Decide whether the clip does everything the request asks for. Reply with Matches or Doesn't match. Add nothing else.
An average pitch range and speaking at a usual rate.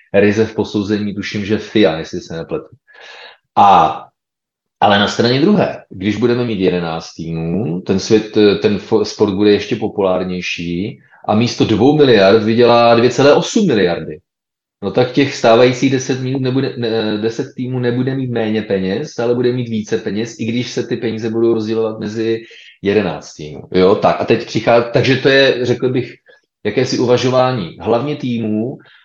Matches